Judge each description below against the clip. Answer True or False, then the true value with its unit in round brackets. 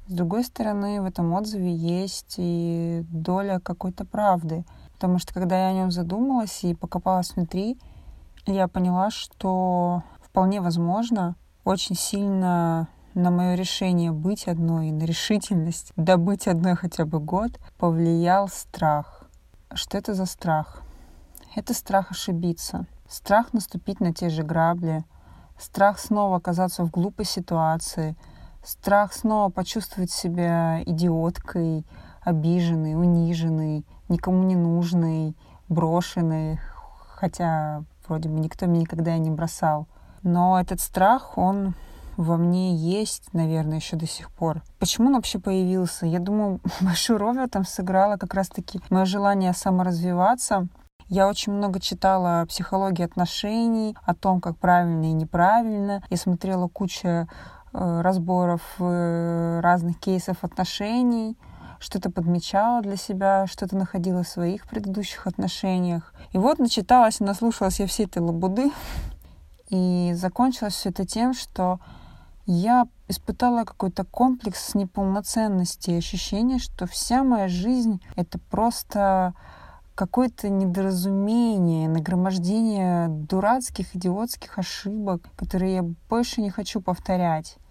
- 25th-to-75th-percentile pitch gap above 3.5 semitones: False (2.7 semitones)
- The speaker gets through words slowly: False (120 wpm)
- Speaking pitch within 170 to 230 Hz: True (185 Hz)